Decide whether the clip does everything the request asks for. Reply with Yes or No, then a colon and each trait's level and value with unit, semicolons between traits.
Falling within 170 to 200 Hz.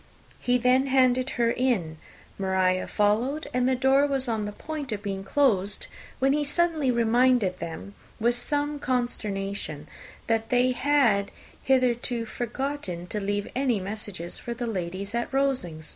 No: high, 240 Hz